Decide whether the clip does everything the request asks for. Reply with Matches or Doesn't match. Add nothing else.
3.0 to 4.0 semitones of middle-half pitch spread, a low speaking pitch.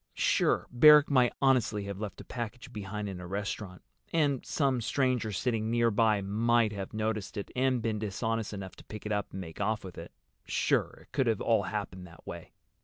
Matches